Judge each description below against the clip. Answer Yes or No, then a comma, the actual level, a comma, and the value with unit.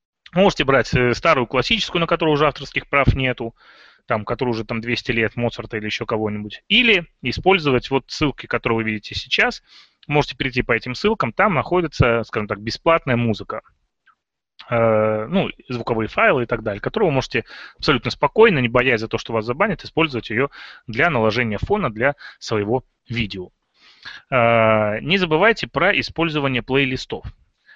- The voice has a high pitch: No, low, 125 Hz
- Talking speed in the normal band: Yes, average, 150 wpm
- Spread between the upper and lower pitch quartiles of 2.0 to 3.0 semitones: No, average, 5.0 semitones